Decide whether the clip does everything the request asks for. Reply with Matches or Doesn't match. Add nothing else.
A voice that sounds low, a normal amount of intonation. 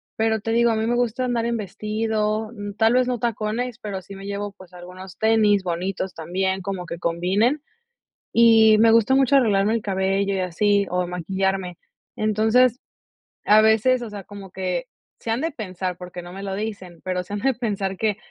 Doesn't match